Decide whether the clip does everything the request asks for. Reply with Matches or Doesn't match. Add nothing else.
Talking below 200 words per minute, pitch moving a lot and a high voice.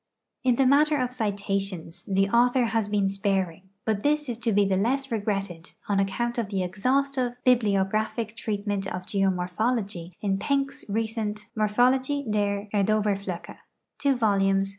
Doesn't match